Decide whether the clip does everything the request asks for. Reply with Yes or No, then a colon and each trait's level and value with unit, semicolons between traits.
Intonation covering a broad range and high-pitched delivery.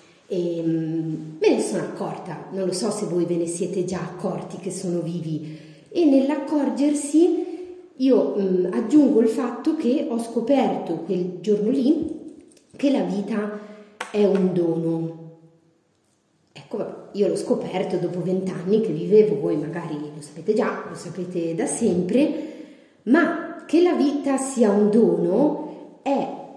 Yes: wide, 7.8 semitones; high, 210 Hz